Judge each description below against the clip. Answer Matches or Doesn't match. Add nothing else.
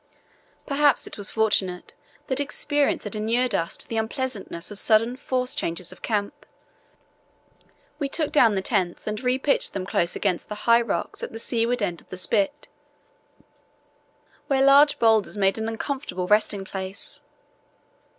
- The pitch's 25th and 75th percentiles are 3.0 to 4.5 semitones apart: Doesn't match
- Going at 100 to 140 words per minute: Doesn't match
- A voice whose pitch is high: Matches